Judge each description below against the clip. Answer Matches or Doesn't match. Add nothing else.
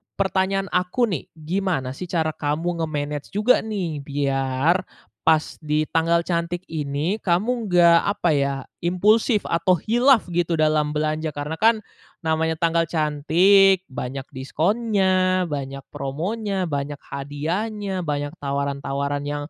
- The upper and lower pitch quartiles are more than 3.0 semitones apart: Matches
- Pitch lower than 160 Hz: Doesn't match